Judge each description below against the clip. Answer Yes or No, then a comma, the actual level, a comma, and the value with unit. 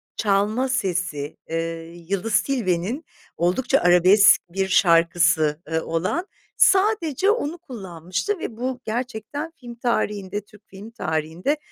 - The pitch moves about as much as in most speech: No, wide, 6.6 semitones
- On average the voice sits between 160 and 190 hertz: No, high, 205 Hz